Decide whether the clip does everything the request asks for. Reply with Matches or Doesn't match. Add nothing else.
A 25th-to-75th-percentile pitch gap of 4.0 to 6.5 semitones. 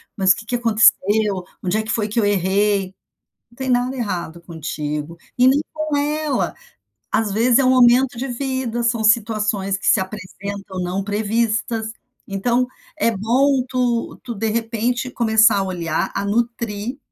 Doesn't match